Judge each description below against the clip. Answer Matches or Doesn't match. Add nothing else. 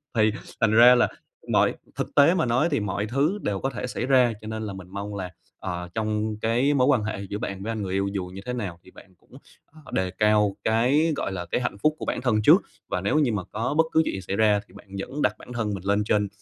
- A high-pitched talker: Doesn't match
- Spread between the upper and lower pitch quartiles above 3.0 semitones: Matches